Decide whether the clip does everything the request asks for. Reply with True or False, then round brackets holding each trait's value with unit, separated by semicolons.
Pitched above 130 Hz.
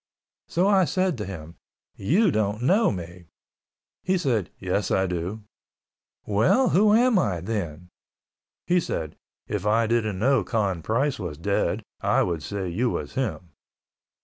False (105 Hz)